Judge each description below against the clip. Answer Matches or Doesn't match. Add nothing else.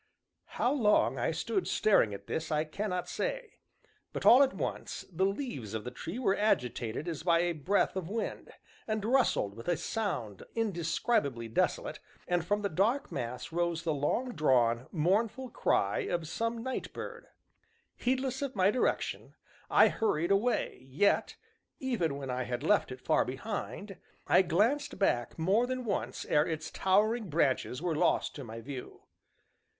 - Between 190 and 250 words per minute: Doesn't match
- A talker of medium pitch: Matches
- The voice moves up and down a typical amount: Doesn't match